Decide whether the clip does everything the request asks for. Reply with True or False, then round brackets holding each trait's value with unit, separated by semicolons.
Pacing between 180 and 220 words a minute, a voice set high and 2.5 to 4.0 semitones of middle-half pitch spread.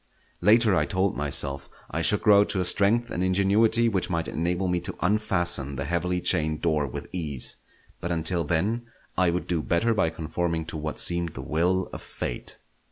False (185 wpm; 85 Hz; 3.4 semitones)